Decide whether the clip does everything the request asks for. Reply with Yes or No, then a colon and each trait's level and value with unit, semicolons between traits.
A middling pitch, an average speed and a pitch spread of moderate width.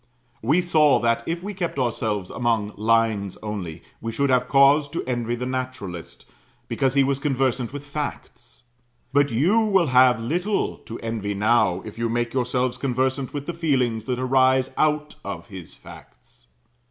No: low, 125 Hz; average, 165 wpm; average, 3.8 semitones